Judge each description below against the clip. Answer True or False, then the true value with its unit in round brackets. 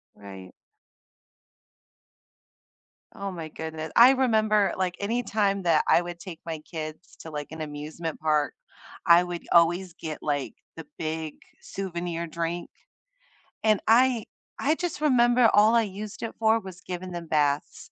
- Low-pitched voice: False (175 Hz)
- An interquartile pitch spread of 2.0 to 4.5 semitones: False (5.1 semitones)